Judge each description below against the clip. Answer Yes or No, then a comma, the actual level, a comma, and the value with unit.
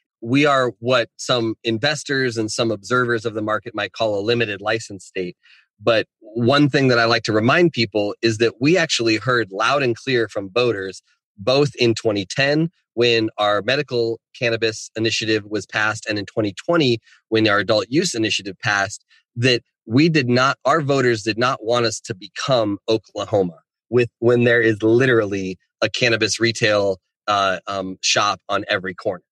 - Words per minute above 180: No, average, 170 wpm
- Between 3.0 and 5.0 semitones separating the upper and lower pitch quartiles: No, narrow, 2.4 semitones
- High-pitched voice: No, low, 115 Hz